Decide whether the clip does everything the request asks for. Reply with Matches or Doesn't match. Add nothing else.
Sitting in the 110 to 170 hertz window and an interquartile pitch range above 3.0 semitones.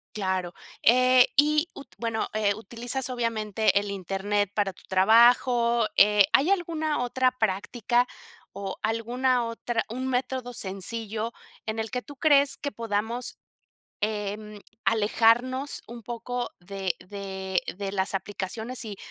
Doesn't match